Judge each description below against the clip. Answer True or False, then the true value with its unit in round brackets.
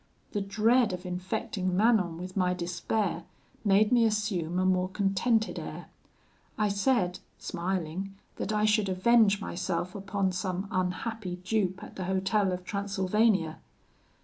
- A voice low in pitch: False (195 Hz)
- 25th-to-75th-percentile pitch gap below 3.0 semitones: True (2.6 semitones)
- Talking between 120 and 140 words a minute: True (135 wpm)